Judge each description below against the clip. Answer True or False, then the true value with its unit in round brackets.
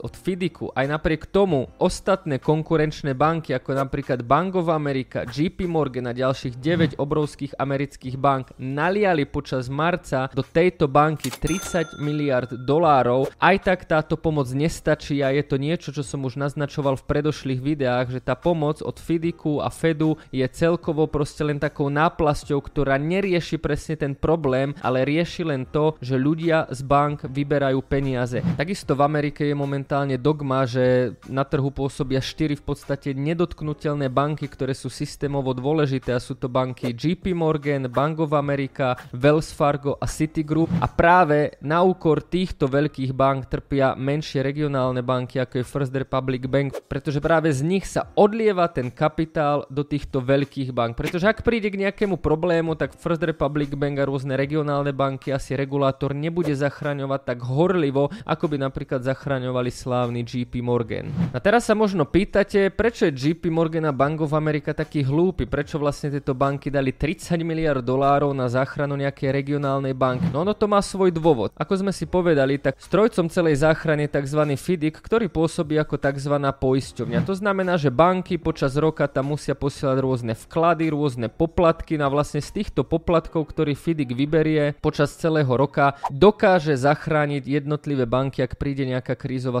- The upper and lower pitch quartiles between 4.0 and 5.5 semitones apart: False (3.0 semitones)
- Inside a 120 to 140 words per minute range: False (165 wpm)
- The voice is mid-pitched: True (145 Hz)